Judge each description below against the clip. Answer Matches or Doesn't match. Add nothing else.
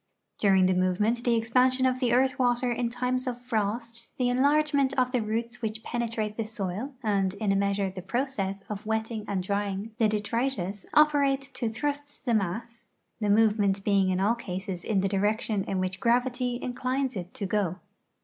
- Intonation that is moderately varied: Matches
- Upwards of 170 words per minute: Matches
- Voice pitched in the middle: Doesn't match